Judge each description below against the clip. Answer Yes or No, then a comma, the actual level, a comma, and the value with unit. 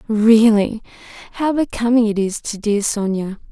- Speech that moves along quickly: No, slow, 135 wpm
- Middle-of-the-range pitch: No, high, 220 Hz